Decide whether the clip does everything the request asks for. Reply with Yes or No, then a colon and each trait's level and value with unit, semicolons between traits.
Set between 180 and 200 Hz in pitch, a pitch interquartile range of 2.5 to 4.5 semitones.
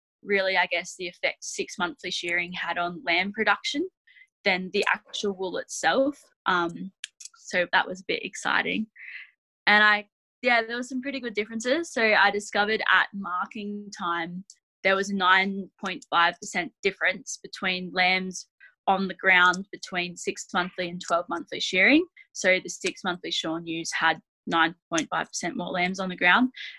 Yes: high, 190 Hz; average, 3.6 semitones